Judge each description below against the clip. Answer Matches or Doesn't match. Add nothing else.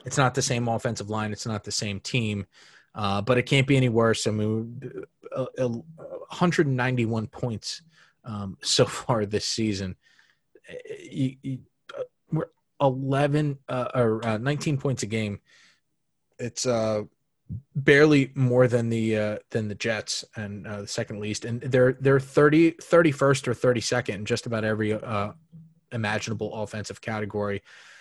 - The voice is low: Matches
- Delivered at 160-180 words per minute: Doesn't match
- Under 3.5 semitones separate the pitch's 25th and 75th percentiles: Doesn't match